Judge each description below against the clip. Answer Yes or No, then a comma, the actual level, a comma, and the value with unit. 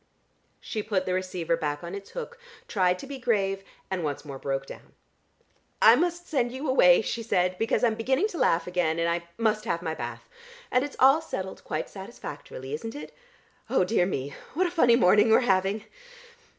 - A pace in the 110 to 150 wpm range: No, average, 195 wpm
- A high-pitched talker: Yes, high, 195 Hz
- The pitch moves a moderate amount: No, wide, 6.0 semitones